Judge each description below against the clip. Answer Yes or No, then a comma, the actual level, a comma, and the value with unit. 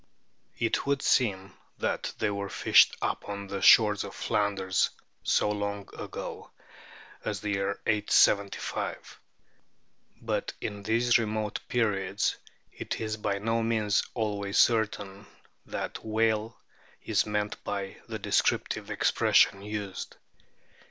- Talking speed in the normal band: No, slow, 120 wpm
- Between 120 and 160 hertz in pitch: No, low, 105 Hz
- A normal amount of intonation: No, narrow, 1.7 semitones